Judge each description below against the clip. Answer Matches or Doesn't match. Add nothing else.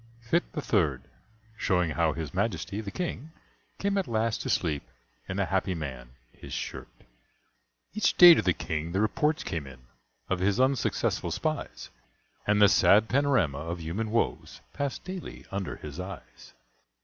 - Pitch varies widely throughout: Matches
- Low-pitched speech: Matches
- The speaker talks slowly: Doesn't match